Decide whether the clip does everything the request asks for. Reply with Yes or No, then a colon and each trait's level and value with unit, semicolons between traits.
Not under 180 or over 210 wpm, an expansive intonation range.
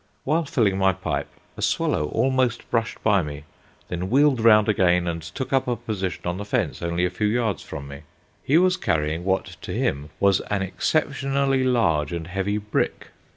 Yes: average, 185 wpm; wide, 6.3 semitones